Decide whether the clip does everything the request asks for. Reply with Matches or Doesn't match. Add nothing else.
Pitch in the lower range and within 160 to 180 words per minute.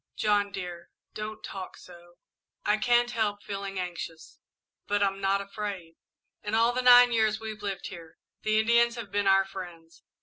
Doesn't match